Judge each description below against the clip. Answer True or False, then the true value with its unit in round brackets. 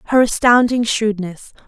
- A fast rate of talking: False (105 wpm)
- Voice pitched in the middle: False (225 Hz)